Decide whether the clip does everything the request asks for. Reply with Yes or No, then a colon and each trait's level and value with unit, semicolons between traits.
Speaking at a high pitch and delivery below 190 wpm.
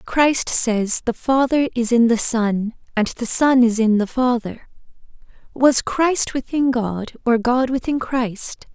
Yes: high, 240 Hz; average, 160 wpm